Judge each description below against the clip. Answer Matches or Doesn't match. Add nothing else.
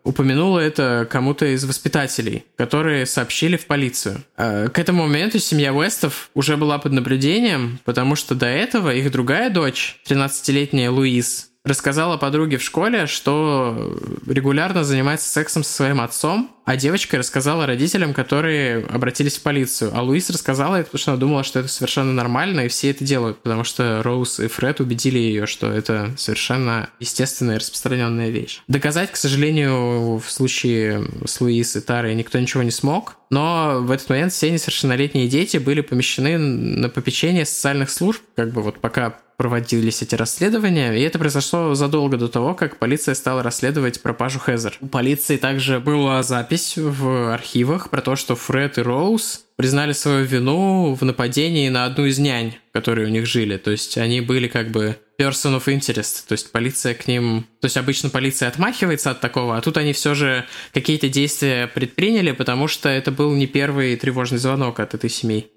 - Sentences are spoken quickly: Matches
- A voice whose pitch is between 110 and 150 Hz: Matches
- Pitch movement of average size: Matches